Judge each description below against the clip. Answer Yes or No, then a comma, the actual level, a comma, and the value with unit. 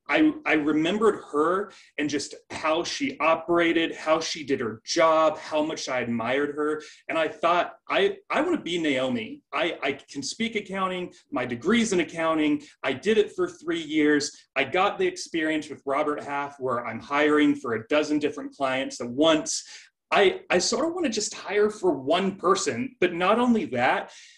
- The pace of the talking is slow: No, average, 185 wpm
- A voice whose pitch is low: No, medium, 170 Hz